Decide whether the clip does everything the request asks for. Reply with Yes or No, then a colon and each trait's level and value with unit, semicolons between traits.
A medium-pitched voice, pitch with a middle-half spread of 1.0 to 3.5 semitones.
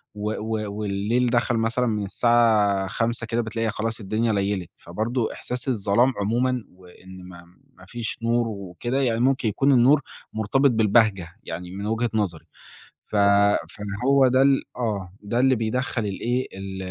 No: low, 110 Hz; average, 3.2 semitones